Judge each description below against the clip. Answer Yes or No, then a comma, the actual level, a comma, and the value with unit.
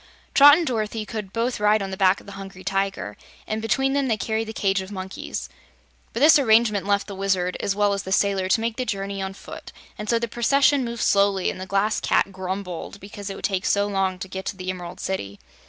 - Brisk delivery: Yes, fast, 235 wpm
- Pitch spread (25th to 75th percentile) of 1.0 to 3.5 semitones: Yes, average, 2.7 semitones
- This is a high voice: Yes, high, 200 Hz